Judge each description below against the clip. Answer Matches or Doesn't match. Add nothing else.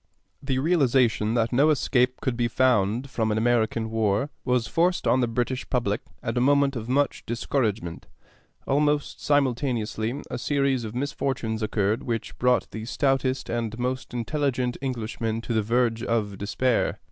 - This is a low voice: Matches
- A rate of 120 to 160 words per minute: Matches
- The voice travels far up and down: Doesn't match